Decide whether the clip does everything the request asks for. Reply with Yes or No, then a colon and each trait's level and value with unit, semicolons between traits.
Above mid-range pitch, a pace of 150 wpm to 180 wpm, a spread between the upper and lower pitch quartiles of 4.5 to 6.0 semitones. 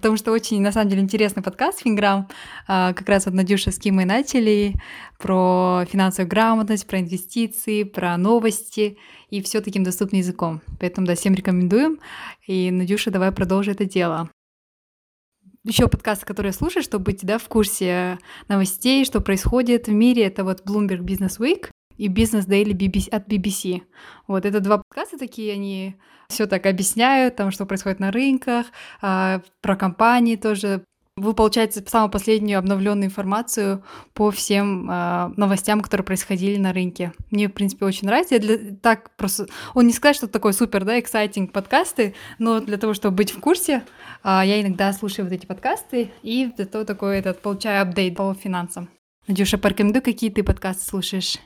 No: high, 205 Hz; fast, 160 wpm; narrow, 2.5 semitones